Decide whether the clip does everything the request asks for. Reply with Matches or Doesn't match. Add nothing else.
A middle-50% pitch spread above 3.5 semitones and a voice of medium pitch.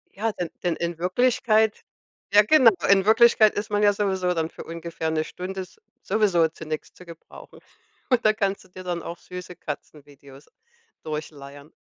Matches